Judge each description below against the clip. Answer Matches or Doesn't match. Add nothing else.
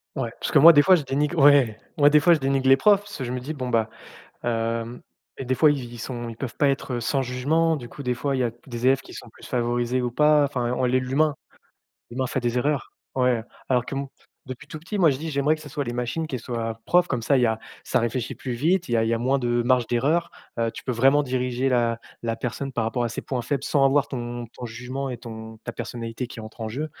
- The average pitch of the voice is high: Doesn't match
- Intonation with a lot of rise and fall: Doesn't match